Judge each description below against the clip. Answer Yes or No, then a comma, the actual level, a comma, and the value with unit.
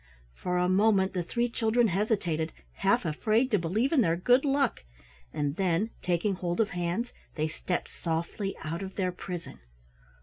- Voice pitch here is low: No, medium, 185 Hz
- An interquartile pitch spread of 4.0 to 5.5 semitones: Yes, average, 4.5 semitones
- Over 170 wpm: No, average, 165 wpm